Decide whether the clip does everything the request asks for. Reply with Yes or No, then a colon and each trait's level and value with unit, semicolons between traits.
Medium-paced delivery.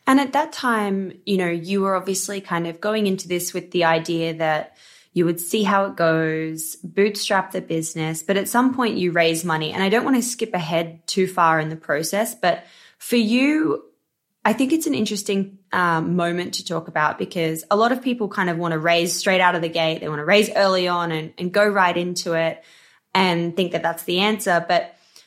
No: fast, 220 wpm